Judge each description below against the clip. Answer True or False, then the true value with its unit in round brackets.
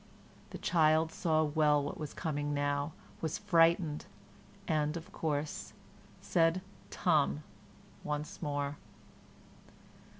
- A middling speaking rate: False (100 wpm)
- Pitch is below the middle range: False (155 Hz)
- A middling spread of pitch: False (1.9 semitones)